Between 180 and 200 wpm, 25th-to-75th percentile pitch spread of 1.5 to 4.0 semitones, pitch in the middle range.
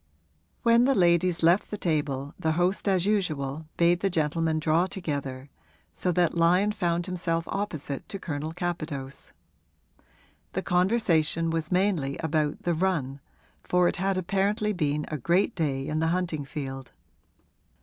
No: average, 145 wpm; average, 3.4 semitones; medium, 170 Hz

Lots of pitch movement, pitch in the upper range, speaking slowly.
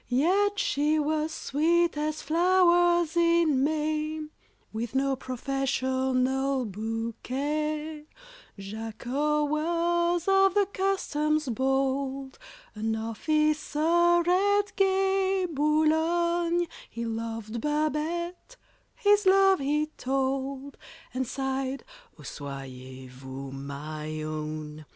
Yes: wide, 5.7 semitones; very high, 300 Hz; slow, 85 wpm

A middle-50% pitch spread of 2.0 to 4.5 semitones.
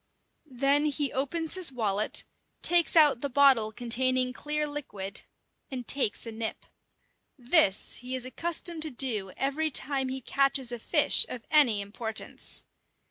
Yes: average, 3.8 semitones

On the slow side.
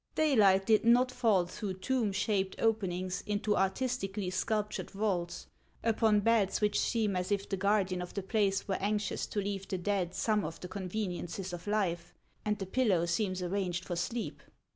No: average, 170 wpm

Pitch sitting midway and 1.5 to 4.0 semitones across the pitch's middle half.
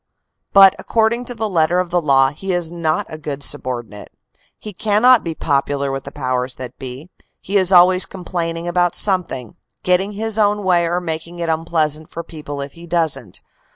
No: medium, 170 Hz; average, 4.4 semitones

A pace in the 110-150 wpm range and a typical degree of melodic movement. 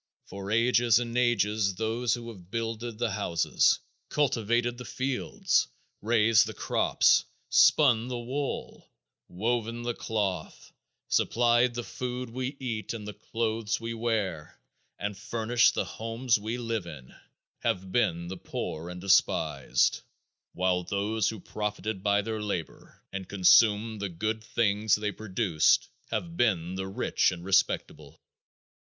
Yes: slow, 135 wpm; average, 3.1 semitones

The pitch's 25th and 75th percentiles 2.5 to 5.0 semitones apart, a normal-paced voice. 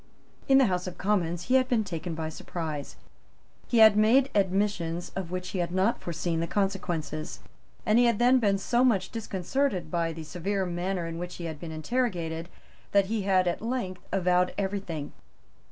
Yes: average, 3.8 semitones; average, 185 wpm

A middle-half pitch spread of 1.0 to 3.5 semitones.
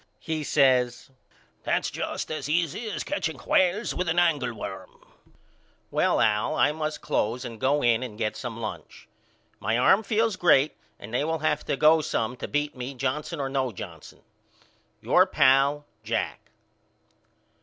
No: average, 4.6 semitones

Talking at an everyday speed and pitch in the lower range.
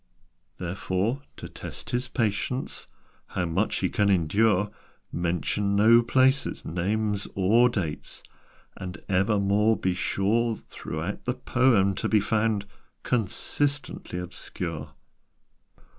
No: slow, 105 wpm; low, 100 Hz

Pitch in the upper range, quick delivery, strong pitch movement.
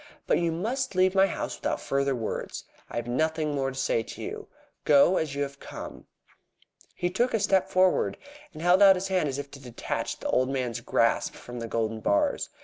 No: medium, 150 Hz; fast, 210 wpm; wide, 6.0 semitones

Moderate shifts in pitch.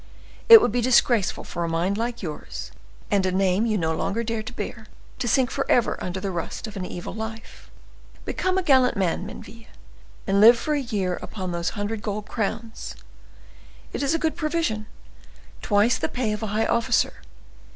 Yes: average, 3.8 semitones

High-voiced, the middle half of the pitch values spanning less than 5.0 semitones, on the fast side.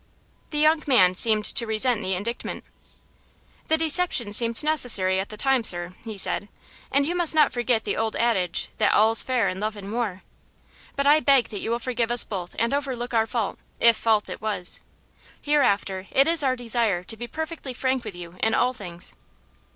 No: high, 230 Hz; average, 4.4 semitones; average, 195 wpm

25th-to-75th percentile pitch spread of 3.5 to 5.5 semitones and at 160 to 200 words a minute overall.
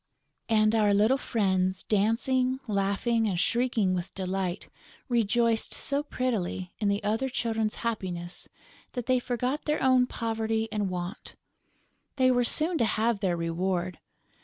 No: average, 4.3 semitones; slow, 135 wpm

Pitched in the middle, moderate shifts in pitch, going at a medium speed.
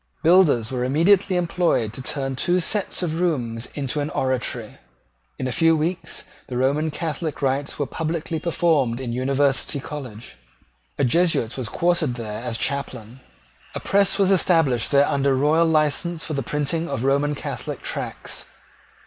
Yes: medium, 145 Hz; average, 4.4 semitones; average, 155 wpm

